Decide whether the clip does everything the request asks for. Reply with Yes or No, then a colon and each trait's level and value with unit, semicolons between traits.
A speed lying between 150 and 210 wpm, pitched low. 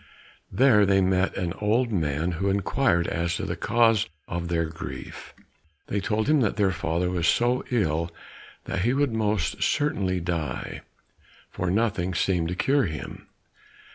Yes: average, 155 wpm; very low, 95 Hz